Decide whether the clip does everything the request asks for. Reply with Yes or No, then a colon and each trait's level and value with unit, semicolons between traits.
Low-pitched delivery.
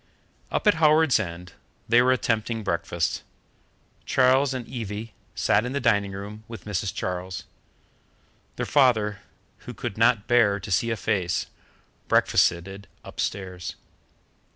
Yes: low, 105 Hz